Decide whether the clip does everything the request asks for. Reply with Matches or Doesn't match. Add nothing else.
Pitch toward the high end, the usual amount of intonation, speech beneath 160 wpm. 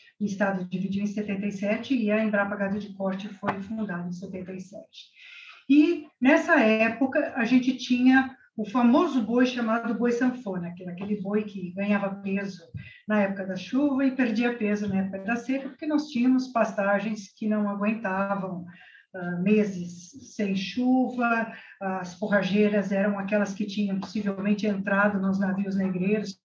Matches